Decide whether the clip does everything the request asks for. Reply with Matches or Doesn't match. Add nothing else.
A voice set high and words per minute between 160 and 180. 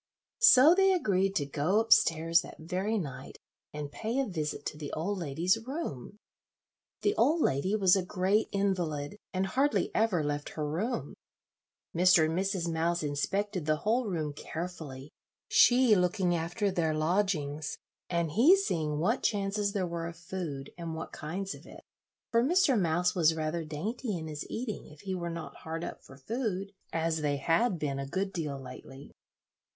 Doesn't match